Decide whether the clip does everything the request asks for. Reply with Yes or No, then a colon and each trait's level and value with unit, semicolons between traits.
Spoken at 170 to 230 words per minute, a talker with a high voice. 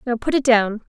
No: fast, 255 wpm; high, 240 Hz